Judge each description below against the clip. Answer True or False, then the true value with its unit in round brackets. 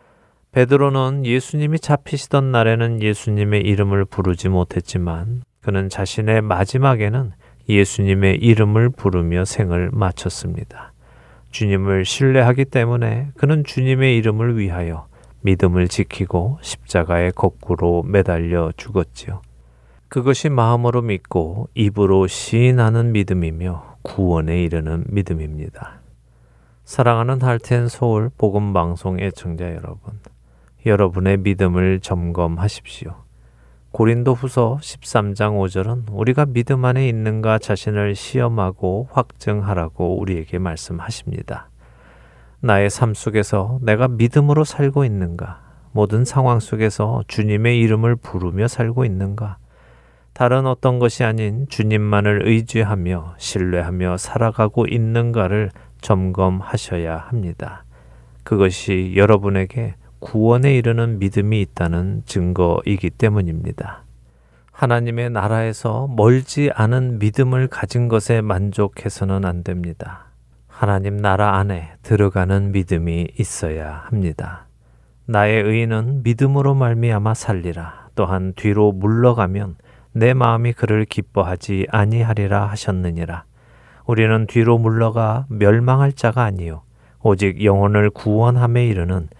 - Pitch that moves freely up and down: False (4.4 semitones)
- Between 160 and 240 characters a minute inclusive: False (285 characters per minute)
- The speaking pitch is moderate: False (105 Hz)